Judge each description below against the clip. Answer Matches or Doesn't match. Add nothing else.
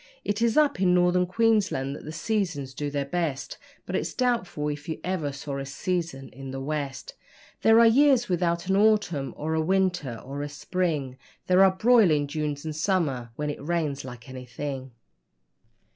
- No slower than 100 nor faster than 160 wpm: Doesn't match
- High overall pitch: Doesn't match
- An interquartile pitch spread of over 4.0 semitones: Matches